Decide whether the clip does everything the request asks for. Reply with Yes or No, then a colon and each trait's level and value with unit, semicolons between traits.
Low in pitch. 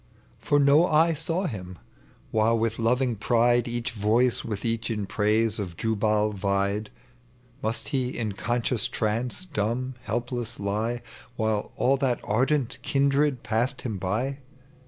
Yes: low, 115 Hz